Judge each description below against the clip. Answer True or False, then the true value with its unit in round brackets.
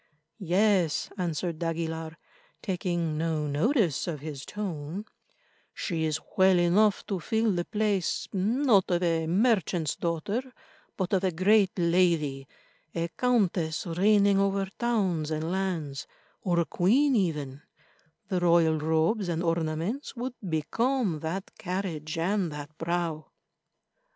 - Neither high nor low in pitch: True (175 Hz)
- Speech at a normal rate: False (120 wpm)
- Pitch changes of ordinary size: True (3.7 semitones)